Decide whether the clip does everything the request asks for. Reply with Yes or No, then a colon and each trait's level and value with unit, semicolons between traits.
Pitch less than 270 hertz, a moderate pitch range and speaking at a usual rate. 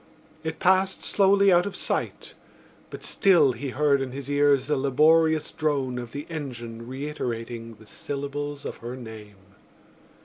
Yes: medium, 140 Hz; average, 4.4 semitones; average, 145 wpm